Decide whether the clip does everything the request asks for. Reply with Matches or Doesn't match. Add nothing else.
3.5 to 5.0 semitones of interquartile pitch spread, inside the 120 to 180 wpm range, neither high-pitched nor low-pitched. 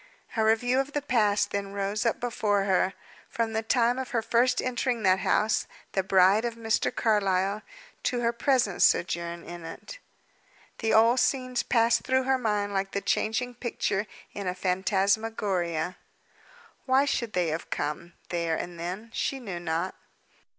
Doesn't match